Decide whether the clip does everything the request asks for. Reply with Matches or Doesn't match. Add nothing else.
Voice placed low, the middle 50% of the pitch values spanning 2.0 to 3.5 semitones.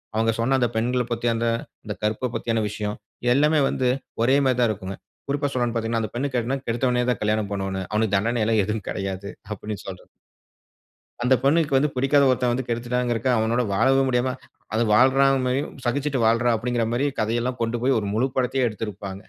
Matches